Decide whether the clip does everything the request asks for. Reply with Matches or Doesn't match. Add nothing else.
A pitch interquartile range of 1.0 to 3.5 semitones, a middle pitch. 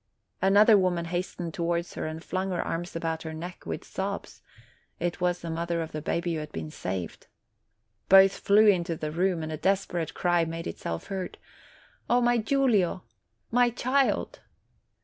Matches